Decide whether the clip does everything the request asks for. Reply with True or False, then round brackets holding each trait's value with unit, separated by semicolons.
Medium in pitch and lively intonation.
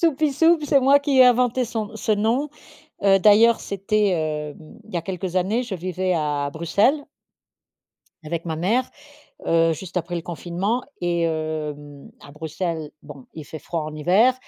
True (180 Hz; 6.1 semitones)